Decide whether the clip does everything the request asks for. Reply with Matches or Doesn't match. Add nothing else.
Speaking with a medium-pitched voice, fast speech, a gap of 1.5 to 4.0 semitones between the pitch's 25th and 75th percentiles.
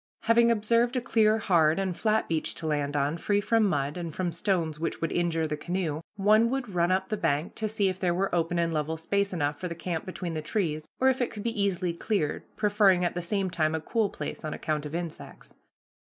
Doesn't match